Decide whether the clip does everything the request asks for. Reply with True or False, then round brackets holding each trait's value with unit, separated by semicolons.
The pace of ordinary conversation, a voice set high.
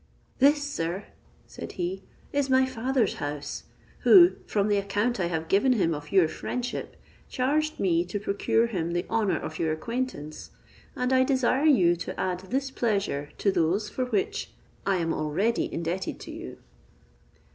True (160 wpm; 200 Hz)